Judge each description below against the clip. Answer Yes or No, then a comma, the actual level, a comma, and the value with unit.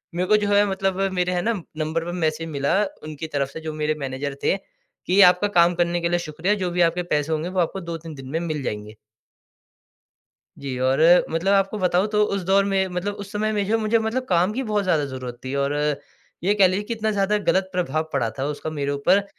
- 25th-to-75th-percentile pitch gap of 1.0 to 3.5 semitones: No, average, 4.4 semitones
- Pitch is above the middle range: No, medium, 175 Hz